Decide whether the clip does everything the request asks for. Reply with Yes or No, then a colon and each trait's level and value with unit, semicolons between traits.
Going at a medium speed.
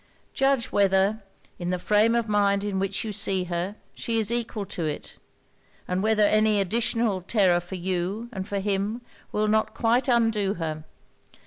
Yes: average, 165 wpm